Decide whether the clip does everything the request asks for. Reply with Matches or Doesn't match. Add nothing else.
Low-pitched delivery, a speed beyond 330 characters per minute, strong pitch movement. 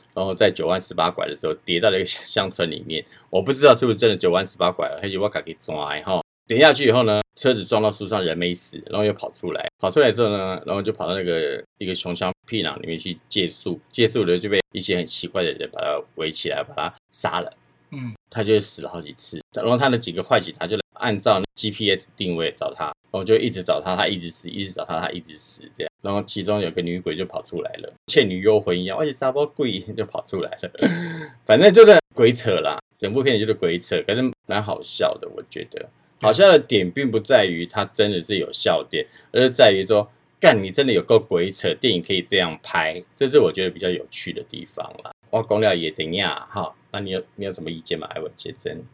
Matches